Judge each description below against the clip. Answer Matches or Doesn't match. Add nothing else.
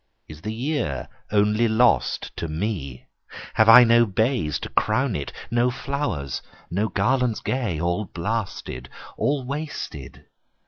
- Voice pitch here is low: Matches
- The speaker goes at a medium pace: Doesn't match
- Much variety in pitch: Matches